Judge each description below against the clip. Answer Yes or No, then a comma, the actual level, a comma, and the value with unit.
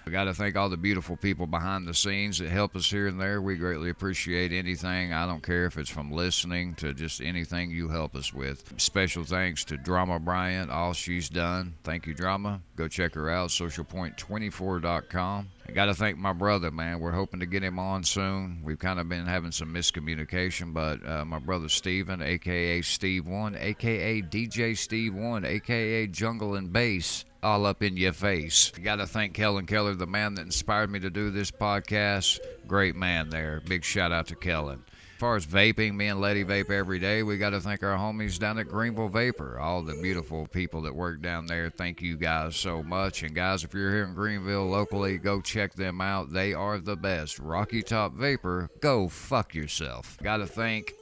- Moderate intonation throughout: Yes, average, 3.1 semitones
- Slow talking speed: No, average, 200 wpm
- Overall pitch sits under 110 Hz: Yes, very low, 95 Hz